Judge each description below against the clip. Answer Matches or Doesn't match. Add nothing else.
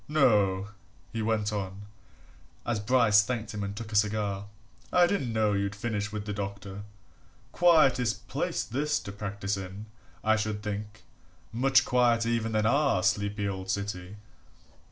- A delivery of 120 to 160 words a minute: Matches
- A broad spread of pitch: Doesn't match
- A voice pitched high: Doesn't match